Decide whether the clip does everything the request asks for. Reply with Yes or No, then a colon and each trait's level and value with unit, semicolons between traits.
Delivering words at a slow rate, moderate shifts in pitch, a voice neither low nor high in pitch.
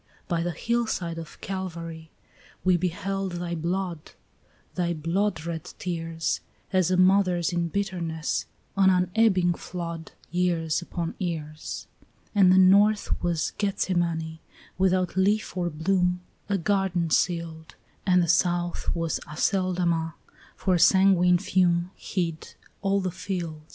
No: slow, 120 wpm; narrow, 2.1 semitones; medium, 175 Hz